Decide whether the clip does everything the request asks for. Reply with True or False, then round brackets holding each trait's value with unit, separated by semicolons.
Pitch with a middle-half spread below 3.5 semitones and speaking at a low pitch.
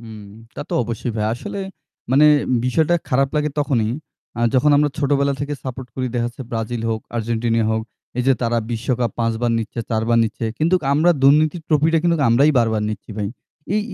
False (4.2 semitones; 125 Hz)